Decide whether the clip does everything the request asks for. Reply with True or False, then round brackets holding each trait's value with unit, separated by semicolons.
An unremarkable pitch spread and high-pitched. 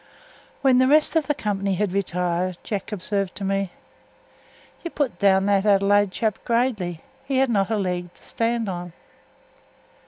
True (3.8 semitones; 200 Hz)